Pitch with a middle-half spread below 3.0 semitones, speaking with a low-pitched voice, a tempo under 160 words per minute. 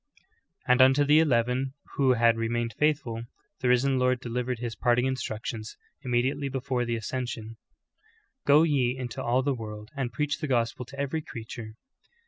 No: narrow, 2.5 semitones; low, 125 Hz; average, 165 wpm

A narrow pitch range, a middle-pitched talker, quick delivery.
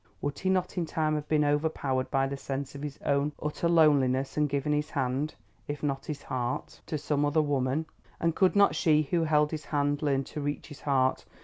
Yes: narrow, 1.9 semitones; medium, 145 Hz; fast, 215 wpm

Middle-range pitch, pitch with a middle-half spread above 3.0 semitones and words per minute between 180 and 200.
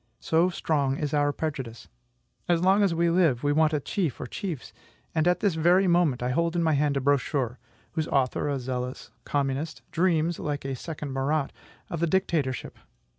Yes: medium, 150 Hz; average, 3.7 semitones; average, 185 wpm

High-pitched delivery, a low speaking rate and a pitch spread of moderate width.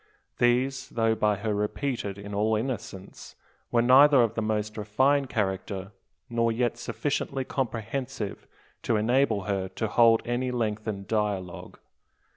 No: low, 110 Hz; slow, 130 wpm; average, 3.0 semitones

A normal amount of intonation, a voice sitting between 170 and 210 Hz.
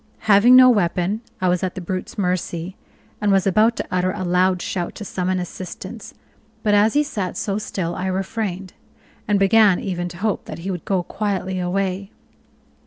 No: narrow, 2.2 semitones; high, 190 Hz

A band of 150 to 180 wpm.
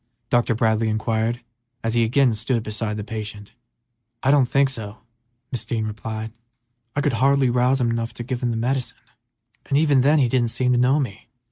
No: average, 195 wpm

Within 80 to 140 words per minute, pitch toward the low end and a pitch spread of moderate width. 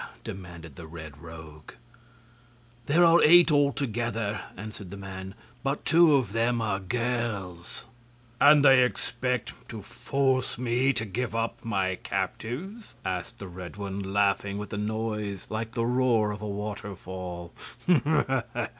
Yes: slow, 135 wpm; low, 110 Hz; average, 4.4 semitones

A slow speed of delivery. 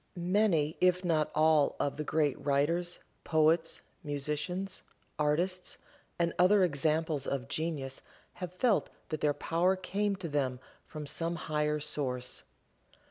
Yes: slow, 130 wpm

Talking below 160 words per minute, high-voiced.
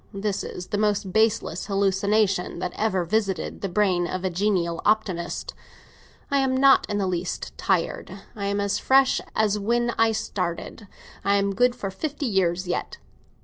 No: average, 165 wpm; high, 200 Hz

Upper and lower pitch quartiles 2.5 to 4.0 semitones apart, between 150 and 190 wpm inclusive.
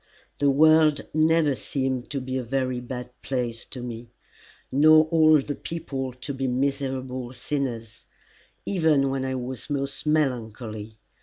No: average, 2.9 semitones; average, 140 wpm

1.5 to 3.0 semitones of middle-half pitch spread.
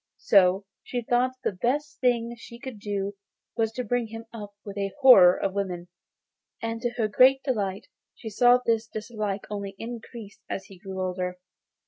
No: average, 3.6 semitones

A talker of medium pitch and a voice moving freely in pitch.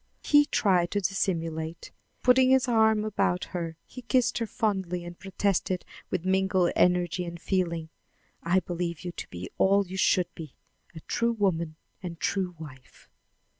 No: medium, 180 Hz; average, 3.1 semitones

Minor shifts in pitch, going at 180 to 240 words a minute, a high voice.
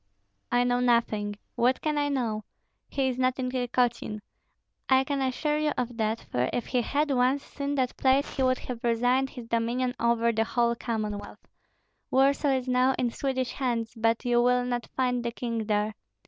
Yes: narrow, 2.1 semitones; average, 185 wpm; high, 245 Hz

